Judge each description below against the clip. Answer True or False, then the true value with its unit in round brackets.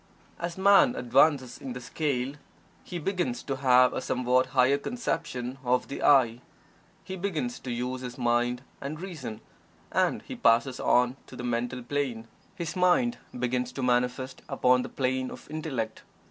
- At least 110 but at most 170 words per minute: True (160 wpm)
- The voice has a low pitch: True (130 Hz)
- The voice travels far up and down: False (3.9 semitones)